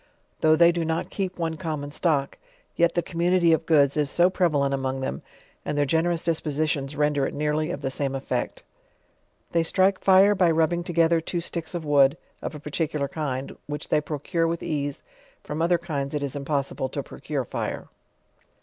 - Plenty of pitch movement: No, average, 3.0 semitones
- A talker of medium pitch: Yes, medium, 155 Hz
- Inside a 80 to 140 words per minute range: No, average, 190 wpm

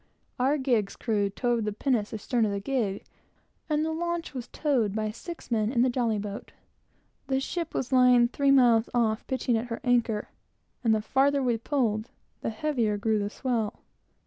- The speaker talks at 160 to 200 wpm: Yes, average, 180 wpm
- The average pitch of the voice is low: No, high, 240 Hz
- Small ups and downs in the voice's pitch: No, average, 3.6 semitones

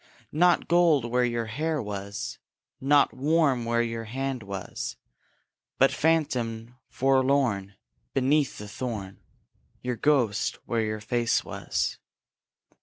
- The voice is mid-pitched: No, low, 125 Hz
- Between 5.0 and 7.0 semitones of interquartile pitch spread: No, average, 4.0 semitones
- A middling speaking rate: No, slow, 110 wpm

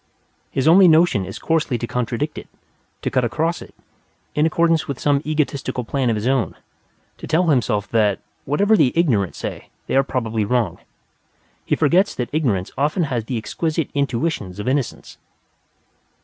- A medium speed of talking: Yes, average, 165 wpm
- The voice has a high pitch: No, low, 135 Hz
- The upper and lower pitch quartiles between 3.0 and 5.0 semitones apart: No, wide, 5.4 semitones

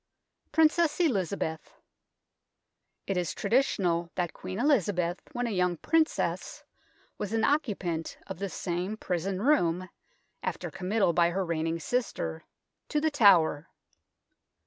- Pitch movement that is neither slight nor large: No, wide, 5.9 semitones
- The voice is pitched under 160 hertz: No, high, 190 Hz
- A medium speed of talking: No, slow, 120 wpm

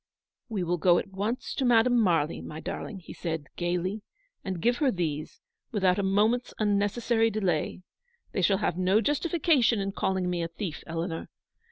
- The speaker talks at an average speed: Yes, average, 175 wpm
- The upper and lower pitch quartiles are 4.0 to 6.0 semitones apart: Yes, average, 4.5 semitones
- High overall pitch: Yes, high, 195 Hz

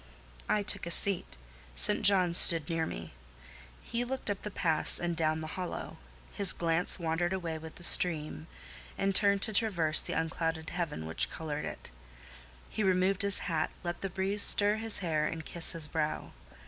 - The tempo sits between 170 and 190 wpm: Yes, average, 175 wpm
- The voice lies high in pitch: No, medium, 175 Hz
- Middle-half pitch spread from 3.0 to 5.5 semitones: Yes, average, 3.5 semitones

